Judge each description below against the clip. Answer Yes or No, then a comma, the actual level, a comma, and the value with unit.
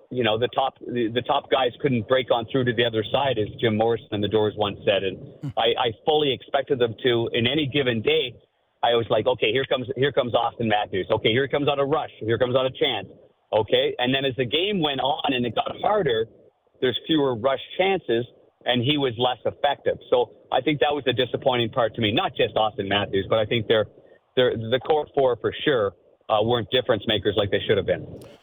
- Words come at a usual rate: No, fast, 230 wpm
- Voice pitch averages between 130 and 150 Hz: Yes, low, 135 Hz